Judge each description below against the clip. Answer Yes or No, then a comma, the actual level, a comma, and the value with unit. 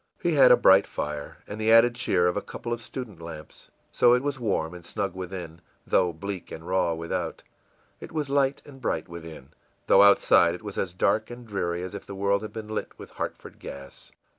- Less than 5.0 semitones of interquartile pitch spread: No, wide, 5.5 semitones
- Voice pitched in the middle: No, low, 100 Hz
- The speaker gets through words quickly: Yes, fast, 215 wpm